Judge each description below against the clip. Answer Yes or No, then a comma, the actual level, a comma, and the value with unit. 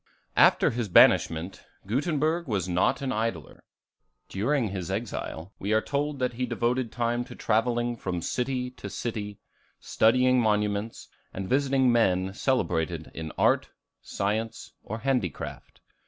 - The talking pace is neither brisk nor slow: No, slow, 130 wpm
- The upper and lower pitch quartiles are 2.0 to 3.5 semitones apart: No, average, 4.6 semitones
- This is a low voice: Yes, low, 115 Hz